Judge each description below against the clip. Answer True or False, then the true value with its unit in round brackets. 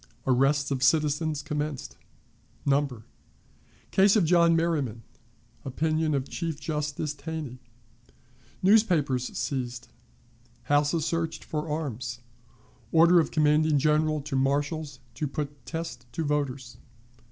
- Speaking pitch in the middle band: True (150 Hz)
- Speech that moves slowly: True (105 wpm)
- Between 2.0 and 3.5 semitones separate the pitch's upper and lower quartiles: True (2.7 semitones)